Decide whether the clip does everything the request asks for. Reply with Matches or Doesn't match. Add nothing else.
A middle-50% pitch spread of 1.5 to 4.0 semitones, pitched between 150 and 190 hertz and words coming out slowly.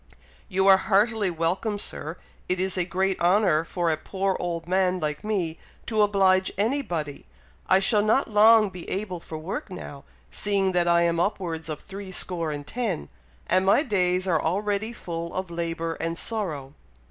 Doesn't match